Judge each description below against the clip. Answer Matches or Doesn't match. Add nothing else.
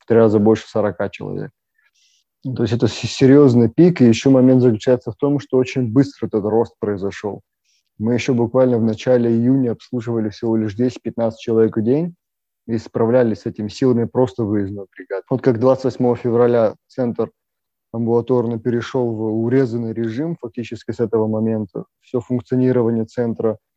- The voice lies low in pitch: Matches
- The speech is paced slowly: Doesn't match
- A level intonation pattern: Matches